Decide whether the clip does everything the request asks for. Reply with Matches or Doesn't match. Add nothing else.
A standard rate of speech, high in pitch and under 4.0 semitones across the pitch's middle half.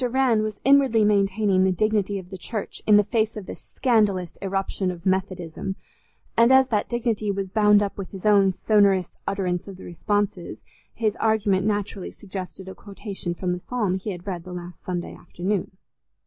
Matches